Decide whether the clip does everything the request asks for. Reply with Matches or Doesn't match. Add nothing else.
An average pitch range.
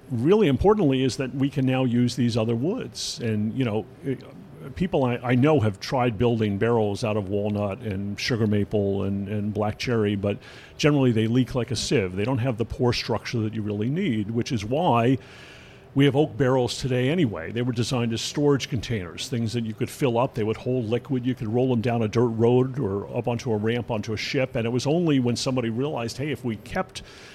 Matches